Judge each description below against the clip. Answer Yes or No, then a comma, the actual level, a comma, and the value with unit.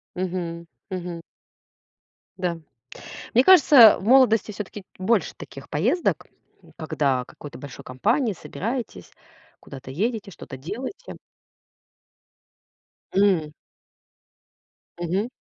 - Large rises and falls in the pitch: Yes, wide, 6.0 semitones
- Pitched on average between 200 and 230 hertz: No, high, 190 Hz